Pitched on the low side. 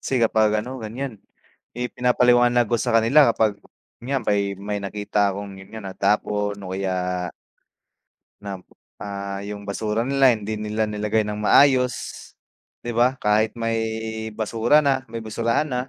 Yes: low, 110 Hz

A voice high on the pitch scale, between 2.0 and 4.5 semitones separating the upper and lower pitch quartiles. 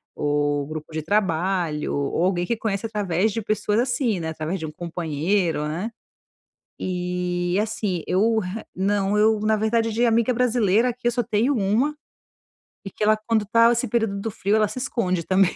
Yes: high, 200 Hz; average, 4.1 semitones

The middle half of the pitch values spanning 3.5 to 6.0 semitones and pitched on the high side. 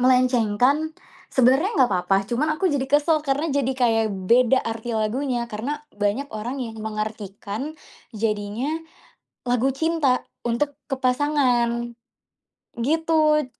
Yes: average, 4.3 semitones; very high, 250 Hz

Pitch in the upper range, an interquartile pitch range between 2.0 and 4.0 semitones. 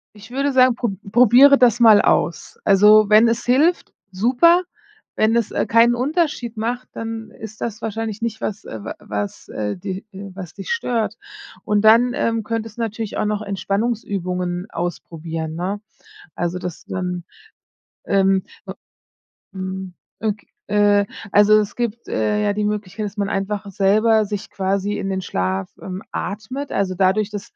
Yes: high, 210 Hz; average, 3.2 semitones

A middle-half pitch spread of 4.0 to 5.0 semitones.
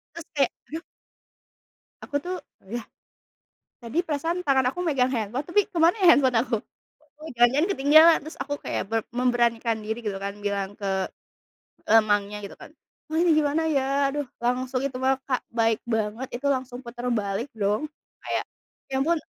Yes: average, 4.7 semitones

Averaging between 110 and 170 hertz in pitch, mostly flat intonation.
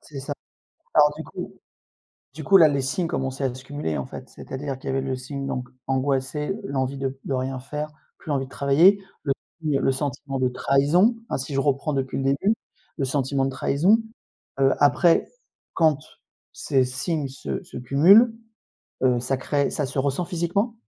Yes: medium, 140 Hz; narrow, 2.3 semitones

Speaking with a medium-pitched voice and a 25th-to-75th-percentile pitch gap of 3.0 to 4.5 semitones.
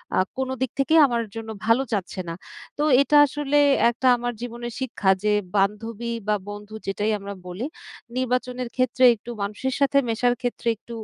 No: high, 235 Hz; average, 3.4 semitones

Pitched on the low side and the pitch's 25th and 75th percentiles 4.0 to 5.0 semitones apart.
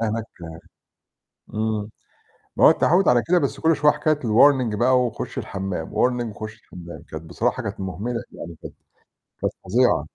Yes: low, 110 Hz; average, 4.7 semitones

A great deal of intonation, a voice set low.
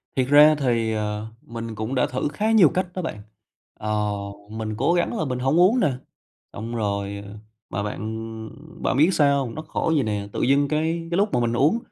Yes: wide, 6.3 semitones; low, 130 Hz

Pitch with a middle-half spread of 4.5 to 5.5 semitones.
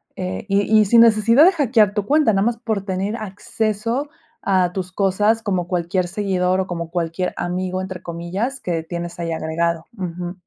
No: average, 3.6 semitones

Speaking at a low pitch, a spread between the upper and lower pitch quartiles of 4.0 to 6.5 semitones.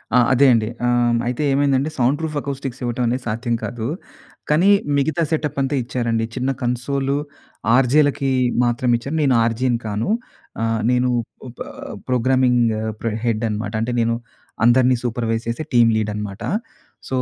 No: low, 125 Hz; average, 2.7 semitones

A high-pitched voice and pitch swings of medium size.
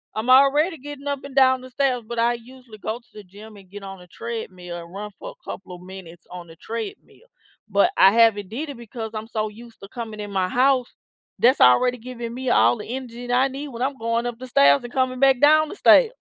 Yes: high, 235 Hz; average, 4.0 semitones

